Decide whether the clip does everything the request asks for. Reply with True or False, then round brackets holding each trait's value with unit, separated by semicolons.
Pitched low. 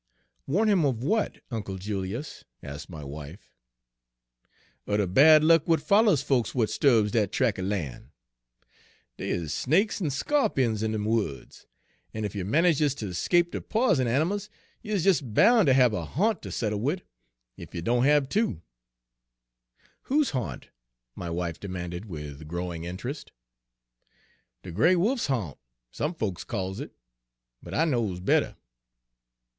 True (115 Hz)